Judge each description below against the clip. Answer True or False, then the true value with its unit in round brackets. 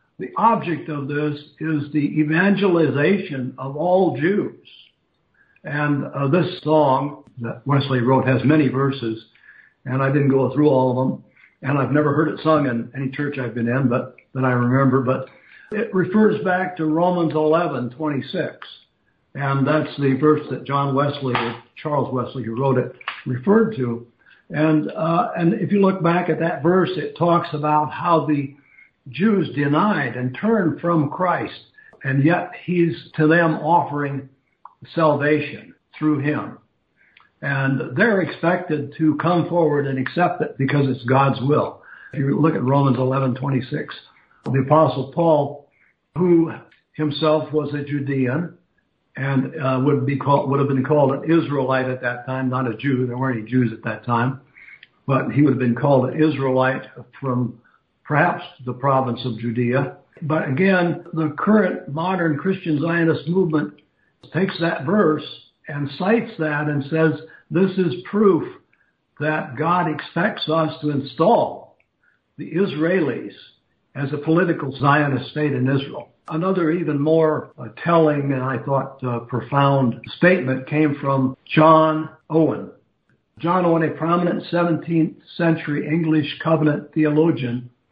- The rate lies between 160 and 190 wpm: False (150 wpm)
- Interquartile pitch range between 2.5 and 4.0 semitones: True (3.5 semitones)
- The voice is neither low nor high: True (150 Hz)